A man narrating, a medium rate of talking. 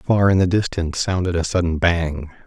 Yes: male; average, 195 wpm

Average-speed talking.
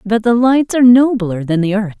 No: fast, 240 wpm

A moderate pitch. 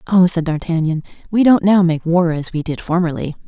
Yes: medium, 170 Hz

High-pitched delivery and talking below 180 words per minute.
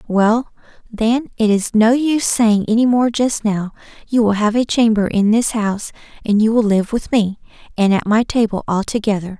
No: high, 220 Hz; average, 190 wpm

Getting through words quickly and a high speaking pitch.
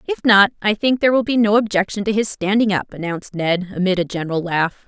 Yes: fast, 235 wpm; high, 200 Hz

